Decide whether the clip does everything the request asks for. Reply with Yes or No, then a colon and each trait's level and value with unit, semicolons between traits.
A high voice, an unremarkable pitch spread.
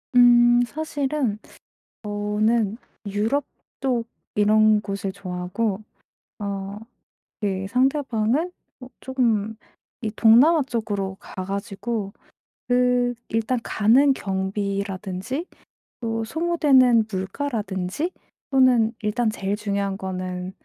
Yes: high, 220 Hz; average, 3.9 semitones